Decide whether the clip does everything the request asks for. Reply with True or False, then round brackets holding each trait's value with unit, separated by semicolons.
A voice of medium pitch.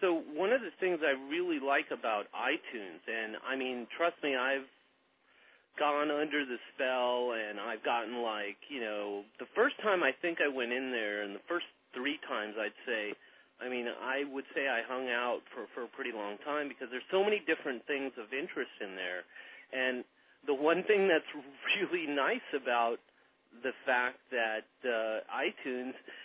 False (130 Hz)